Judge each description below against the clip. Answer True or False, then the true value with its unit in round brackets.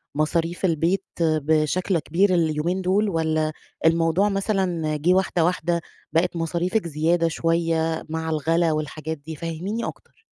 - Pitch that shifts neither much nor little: False (2.2 semitones)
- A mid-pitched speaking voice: True (165 Hz)